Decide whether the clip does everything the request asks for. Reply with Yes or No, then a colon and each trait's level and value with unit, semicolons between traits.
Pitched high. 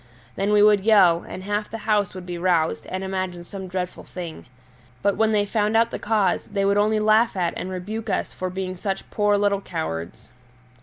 Yes: high, 195 Hz